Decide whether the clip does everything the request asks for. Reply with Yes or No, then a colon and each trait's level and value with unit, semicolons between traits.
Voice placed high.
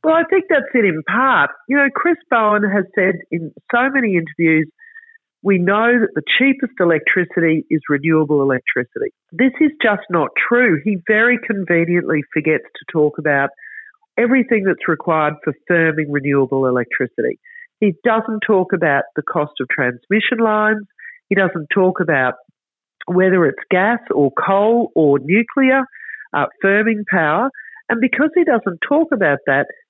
Yes: high, 200 Hz